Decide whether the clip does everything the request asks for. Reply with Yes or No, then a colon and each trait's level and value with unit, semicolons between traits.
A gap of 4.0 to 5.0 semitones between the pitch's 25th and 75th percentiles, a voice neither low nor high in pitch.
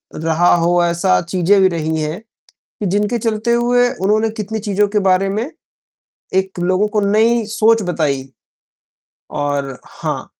No: average, 4.3 semitones; high, 195 Hz